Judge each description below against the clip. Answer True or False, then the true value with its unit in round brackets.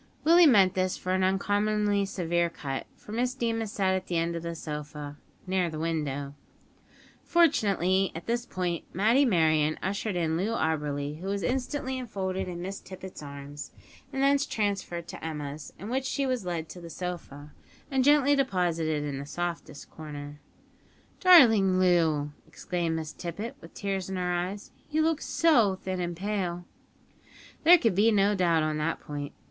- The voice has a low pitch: False (185 Hz)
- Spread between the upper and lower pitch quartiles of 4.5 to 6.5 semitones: True (4.8 semitones)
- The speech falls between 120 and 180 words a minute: True (170 wpm)